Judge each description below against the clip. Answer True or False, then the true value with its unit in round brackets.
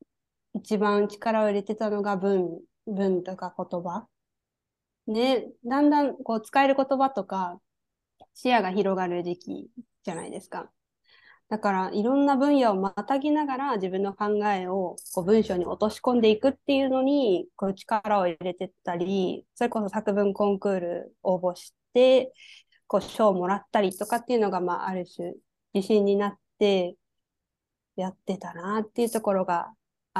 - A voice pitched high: True (205 Hz)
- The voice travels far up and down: False (4.2 semitones)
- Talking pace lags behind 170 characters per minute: False (300 characters per minute)